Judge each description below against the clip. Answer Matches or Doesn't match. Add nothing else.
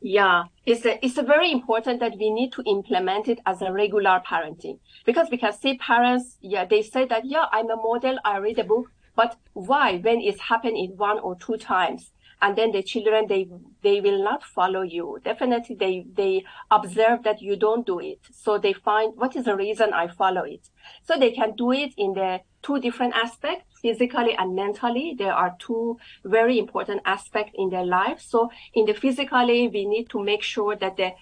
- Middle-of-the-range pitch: Doesn't match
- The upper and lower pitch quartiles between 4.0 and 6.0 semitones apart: Doesn't match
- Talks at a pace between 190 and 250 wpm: Matches